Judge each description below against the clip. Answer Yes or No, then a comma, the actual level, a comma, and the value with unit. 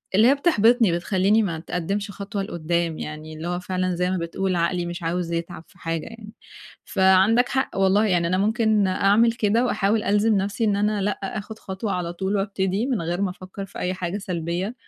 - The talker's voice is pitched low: No, high, 190 Hz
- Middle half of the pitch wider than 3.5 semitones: No, average, 3.1 semitones